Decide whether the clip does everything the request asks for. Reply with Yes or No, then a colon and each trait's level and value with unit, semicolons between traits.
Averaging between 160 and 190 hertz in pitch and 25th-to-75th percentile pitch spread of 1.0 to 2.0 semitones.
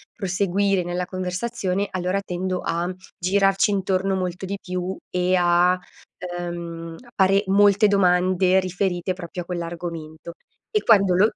Yes: medium, 185 Hz; narrow, 1.7 semitones